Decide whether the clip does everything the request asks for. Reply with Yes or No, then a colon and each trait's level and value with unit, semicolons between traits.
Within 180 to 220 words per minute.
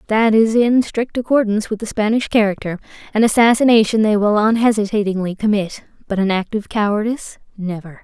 No: average, 155 wpm